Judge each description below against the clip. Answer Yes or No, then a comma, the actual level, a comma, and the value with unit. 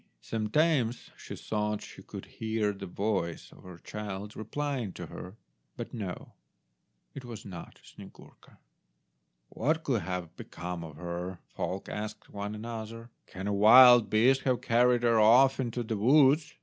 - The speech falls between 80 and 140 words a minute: No, average, 150 wpm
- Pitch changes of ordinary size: Yes, average, 3.9 semitones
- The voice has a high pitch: No, low, 110 Hz